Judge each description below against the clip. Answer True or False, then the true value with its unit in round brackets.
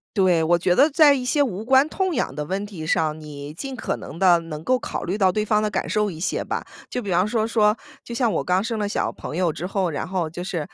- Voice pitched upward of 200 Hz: False (190 Hz)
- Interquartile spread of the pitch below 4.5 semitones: False (5.3 semitones)